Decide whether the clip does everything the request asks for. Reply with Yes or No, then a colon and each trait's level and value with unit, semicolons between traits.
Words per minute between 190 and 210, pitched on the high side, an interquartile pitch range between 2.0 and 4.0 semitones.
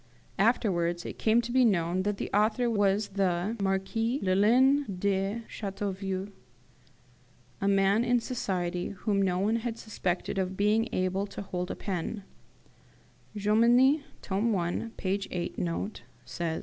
No: slow, 135 wpm; high, 200 Hz; average, 3.3 semitones